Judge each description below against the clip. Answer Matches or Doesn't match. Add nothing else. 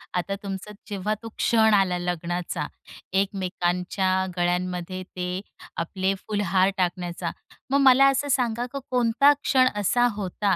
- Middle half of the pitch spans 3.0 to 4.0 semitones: Matches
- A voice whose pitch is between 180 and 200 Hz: Matches